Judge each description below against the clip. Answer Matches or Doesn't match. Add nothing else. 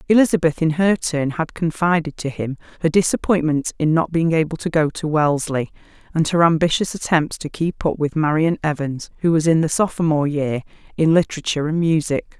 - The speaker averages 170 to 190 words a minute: Matches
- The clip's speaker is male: Doesn't match